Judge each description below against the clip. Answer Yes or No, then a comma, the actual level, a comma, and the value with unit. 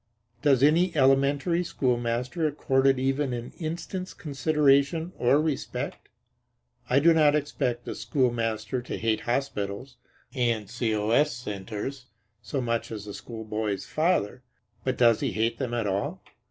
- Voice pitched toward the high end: No, low, 130 Hz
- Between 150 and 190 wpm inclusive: No, slow, 135 wpm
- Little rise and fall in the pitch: No, average, 4.1 semitones